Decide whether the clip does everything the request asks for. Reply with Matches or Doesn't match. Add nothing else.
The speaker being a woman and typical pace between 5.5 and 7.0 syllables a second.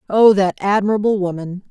Matches